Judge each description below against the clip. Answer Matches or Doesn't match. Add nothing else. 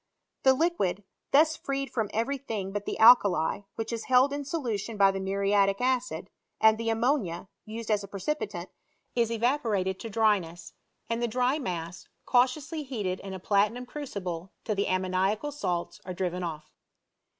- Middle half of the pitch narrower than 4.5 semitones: Doesn't match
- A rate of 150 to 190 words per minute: Matches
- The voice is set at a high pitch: Matches